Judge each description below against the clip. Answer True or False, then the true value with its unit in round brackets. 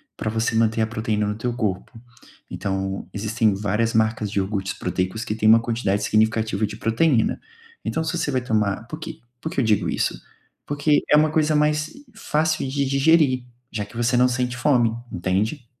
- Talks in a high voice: False (115 Hz)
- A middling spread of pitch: True (4.5 semitones)